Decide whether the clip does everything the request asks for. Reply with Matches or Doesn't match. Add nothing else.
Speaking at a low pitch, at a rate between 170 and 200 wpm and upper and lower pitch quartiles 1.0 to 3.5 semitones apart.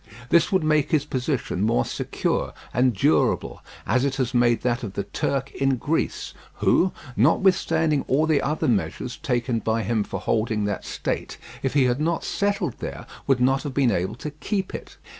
Doesn't match